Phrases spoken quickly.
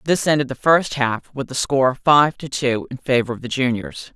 Yes: fast, 230 wpm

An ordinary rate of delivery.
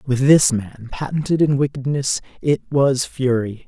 Yes: average, 145 wpm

